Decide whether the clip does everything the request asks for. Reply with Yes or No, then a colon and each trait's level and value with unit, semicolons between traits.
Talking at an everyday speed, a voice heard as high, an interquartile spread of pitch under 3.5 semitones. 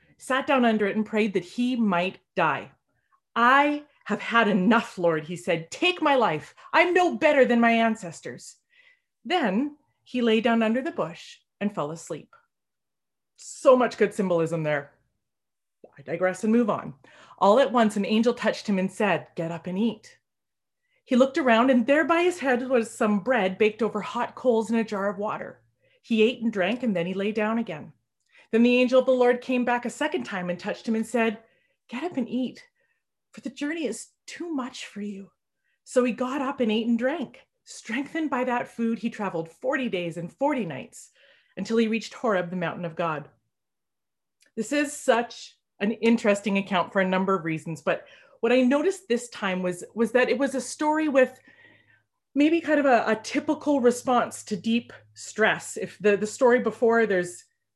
No: average, 190 wpm; high, 230 Hz; average, 4.9 semitones